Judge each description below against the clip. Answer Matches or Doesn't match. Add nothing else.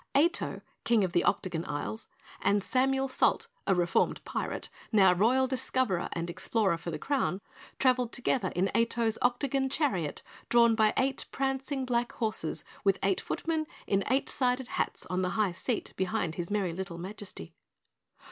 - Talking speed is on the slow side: Doesn't match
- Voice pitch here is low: Doesn't match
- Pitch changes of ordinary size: Doesn't match